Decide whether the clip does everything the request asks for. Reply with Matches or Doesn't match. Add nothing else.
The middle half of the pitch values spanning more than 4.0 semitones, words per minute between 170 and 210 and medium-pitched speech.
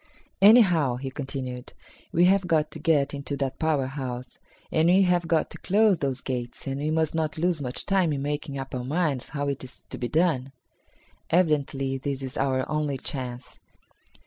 Doesn't match